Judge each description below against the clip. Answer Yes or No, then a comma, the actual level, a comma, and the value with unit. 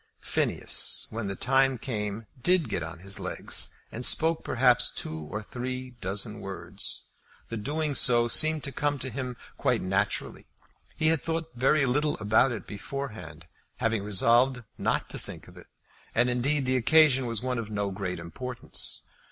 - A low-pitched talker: Yes, low, 120 Hz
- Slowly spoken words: No, average, 165 wpm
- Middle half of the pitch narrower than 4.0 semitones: No, average, 4.6 semitones